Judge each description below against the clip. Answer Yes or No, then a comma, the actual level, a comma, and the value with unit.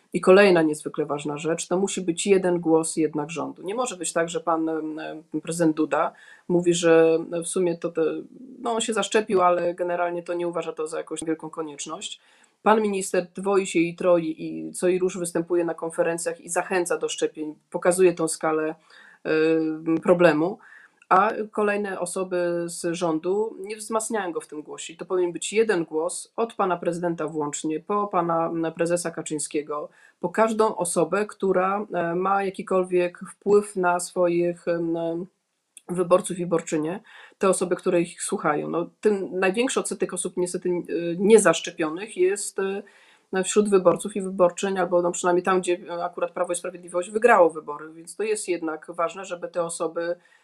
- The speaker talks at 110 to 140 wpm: No, fast, 160 wpm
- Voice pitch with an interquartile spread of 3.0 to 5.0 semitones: No, narrow, 2.5 semitones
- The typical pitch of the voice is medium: Yes, medium, 175 Hz